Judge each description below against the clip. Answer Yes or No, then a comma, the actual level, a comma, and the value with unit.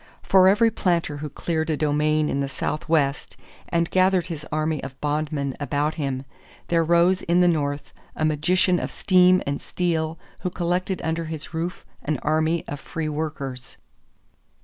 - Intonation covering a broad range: No, average, 2.8 semitones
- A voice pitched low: No, medium, 160 Hz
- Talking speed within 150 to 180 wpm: Yes, average, 160 wpm